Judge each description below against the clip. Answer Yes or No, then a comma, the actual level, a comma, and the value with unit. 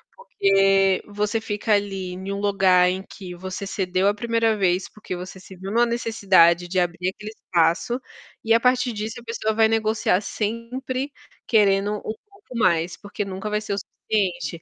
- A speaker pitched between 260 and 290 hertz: No, high, 200 Hz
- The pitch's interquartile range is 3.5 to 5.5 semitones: No, average, 3.1 semitones